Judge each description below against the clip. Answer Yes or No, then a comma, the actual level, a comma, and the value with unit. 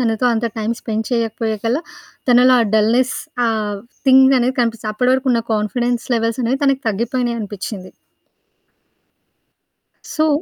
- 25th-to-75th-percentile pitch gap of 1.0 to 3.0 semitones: Yes, narrow, 2.4 semitones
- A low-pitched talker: No, high, 235 Hz